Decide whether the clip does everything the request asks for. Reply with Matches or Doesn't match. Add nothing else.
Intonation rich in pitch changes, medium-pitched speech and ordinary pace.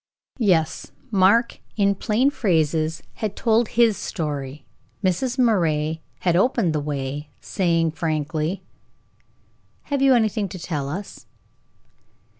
Doesn't match